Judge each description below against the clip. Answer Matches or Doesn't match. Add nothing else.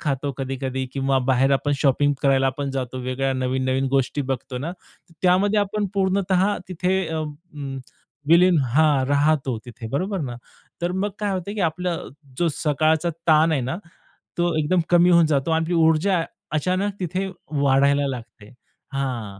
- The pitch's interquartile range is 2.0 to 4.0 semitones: Doesn't match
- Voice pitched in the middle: Matches